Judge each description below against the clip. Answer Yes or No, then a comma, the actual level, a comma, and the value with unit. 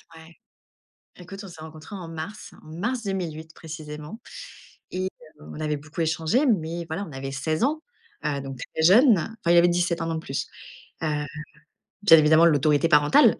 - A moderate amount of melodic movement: Yes, average, 3.1 semitones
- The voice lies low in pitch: No, medium, 160 Hz